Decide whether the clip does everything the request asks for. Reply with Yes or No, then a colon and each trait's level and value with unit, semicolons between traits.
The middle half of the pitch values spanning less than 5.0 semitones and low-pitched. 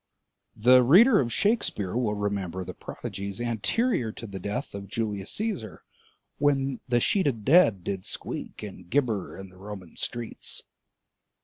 No: average, 5.3 semitones; low, 110 Hz